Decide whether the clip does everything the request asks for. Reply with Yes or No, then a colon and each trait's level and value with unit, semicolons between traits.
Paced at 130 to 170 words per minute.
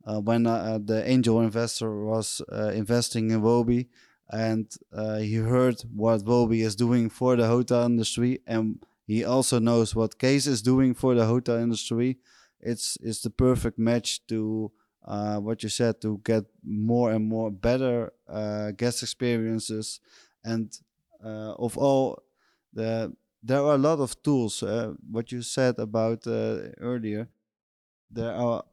Yes: average, 155 wpm